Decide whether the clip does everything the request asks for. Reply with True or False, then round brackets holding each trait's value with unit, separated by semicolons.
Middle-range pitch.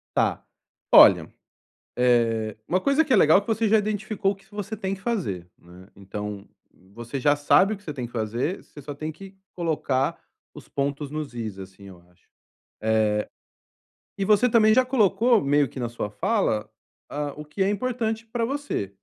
True (150 Hz)